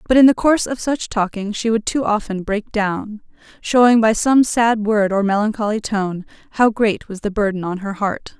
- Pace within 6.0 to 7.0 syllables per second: No, 4.9 syllables/s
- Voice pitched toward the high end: Yes, high, 215 Hz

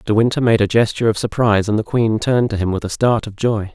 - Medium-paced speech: No, fast, 290 wpm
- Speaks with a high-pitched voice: No, low, 110 Hz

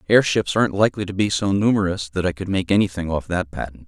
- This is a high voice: No, very low, 95 Hz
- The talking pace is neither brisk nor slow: No, fast, 230 wpm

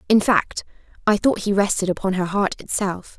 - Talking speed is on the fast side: No, average, 190 wpm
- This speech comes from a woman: Yes, female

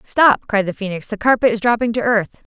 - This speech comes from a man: No, female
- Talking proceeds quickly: Yes, fast, 230 wpm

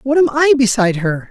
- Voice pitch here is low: No, high, 215 Hz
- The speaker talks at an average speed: No, fast, 230 wpm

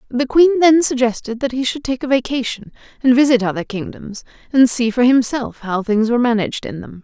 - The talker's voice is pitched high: Yes, high, 245 Hz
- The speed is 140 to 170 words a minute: No, fast, 205 wpm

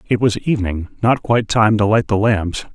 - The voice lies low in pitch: Yes, low, 105 Hz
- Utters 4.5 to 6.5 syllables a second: Yes, 5.2 syllables/s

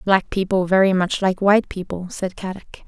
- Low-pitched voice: No, high, 190 Hz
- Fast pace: No, average, 190 wpm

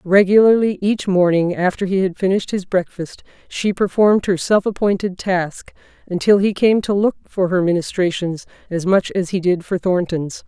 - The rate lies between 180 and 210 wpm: No, average, 170 wpm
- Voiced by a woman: Yes, female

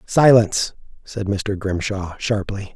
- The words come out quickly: No, slow, 110 wpm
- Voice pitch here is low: Yes, low, 100 Hz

